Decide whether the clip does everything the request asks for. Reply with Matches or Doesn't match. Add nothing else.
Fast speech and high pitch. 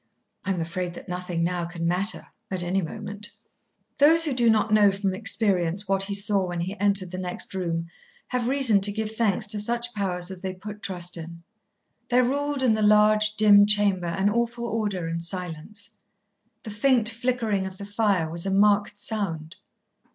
Doesn't match